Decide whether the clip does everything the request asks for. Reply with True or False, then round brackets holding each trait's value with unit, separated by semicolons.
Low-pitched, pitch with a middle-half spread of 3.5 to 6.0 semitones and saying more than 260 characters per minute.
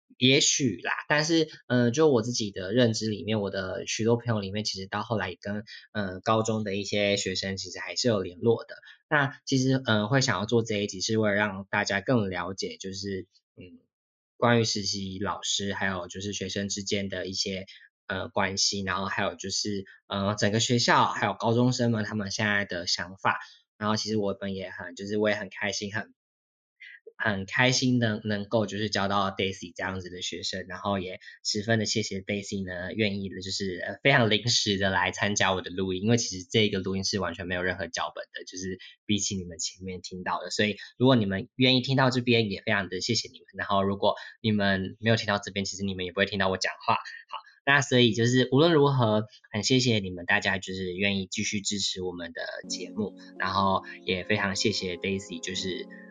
False (100 Hz; 2.9 semitones; 325 characters per minute)